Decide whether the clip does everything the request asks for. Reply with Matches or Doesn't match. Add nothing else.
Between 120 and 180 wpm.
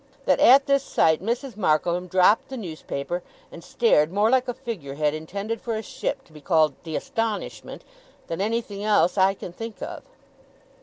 Matches